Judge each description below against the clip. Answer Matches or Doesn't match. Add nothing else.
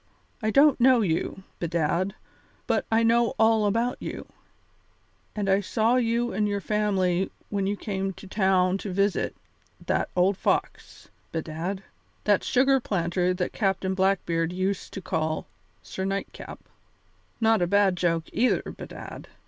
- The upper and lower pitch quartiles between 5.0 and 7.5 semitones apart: Doesn't match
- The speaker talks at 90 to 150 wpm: Matches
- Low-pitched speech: Doesn't match